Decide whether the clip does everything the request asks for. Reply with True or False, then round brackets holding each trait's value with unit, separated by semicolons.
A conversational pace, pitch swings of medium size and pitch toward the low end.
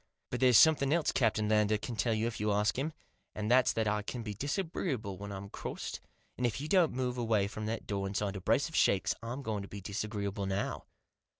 False (225 wpm; 3.7 semitones; 110 Hz)